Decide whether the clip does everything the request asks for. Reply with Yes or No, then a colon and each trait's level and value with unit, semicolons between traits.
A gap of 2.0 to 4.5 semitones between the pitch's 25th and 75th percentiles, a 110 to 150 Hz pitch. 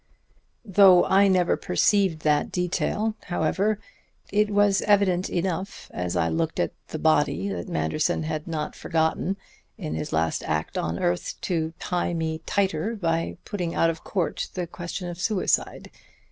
No: average, 3.8 semitones; medium, 175 Hz